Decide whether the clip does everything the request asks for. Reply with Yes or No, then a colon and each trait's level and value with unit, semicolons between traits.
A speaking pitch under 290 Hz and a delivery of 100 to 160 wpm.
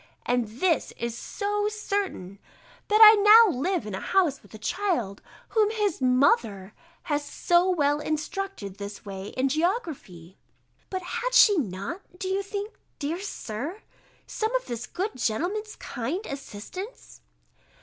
No: very high, 330 Hz; average, 140 wpm